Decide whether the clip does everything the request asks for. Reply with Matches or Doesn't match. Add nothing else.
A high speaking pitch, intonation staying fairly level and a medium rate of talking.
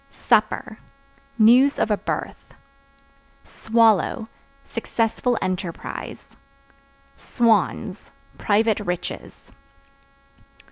Doesn't match